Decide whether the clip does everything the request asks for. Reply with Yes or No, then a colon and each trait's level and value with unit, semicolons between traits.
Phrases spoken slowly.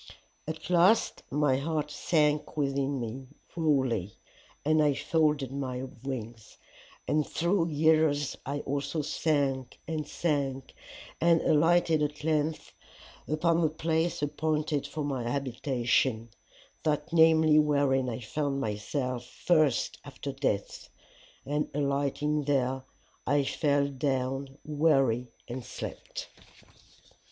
Yes: slow, 110 wpm